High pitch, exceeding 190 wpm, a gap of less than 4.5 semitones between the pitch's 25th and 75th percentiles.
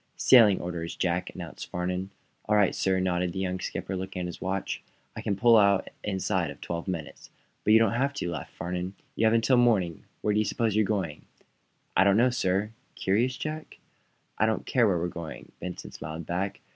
No: very low, 95 Hz; average, 200 wpm; average, 3.6 semitones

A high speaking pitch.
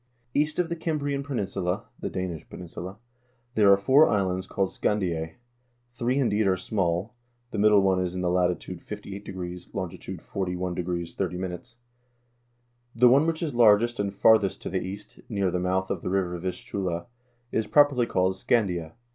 No: very low, 95 Hz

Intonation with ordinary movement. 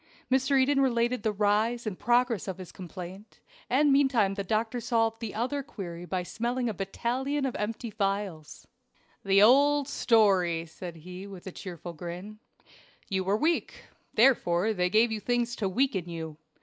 Yes: average, 4.6 semitones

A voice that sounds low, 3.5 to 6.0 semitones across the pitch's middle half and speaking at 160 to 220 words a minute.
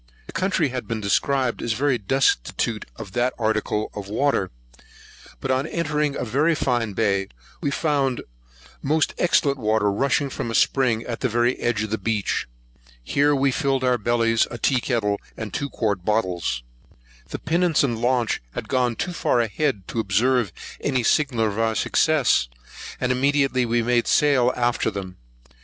Yes: low, 120 Hz; average, 4.0 semitones; average, 165 wpm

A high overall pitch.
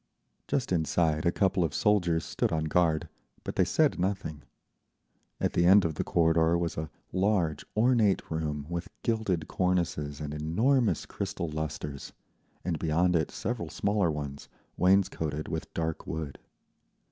No: very low, 85 Hz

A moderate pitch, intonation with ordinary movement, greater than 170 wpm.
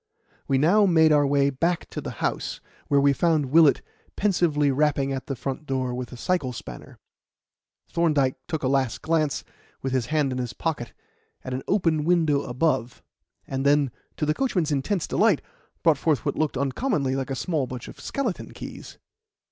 Yes: medium, 145 Hz; average, 3.5 semitones; average, 180 wpm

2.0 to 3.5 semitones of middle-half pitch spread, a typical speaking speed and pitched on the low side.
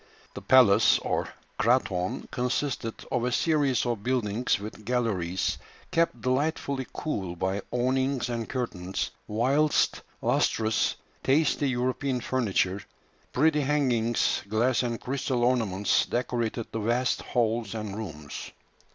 No: average, 3.2 semitones; slow, 115 wpm; low, 120 Hz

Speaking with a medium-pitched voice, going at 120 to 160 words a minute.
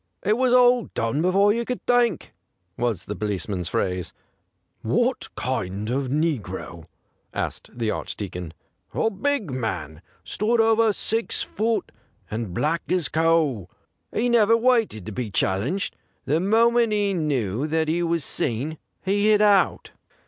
Yes: medium, 160 Hz; average, 155 wpm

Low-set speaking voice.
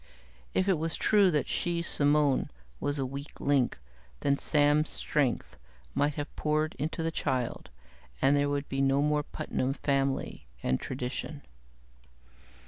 No: medium, 145 Hz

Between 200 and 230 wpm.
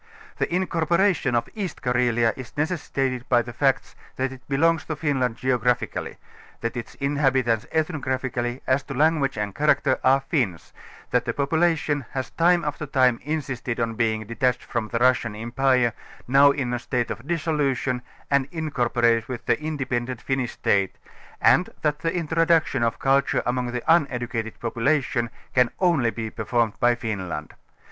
No: average, 155 wpm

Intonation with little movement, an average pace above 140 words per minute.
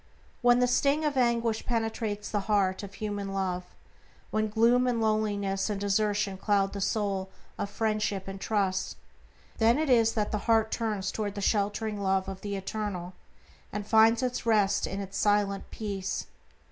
Yes: narrow, 2.2 semitones; average, 160 wpm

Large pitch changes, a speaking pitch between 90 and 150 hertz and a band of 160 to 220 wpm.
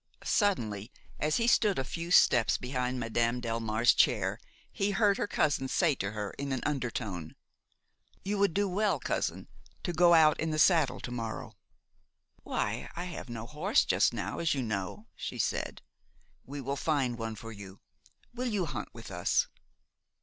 Yes: wide, 7.2 semitones; low, 135 Hz; average, 170 wpm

